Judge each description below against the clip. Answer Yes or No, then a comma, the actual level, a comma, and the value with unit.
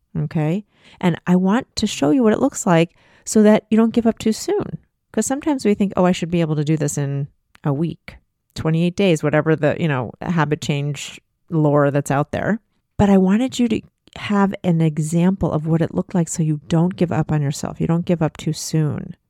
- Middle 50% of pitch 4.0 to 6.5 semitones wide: Yes, average, 4.5 semitones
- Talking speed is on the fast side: Yes, fast, 225 wpm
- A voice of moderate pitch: Yes, medium, 170 Hz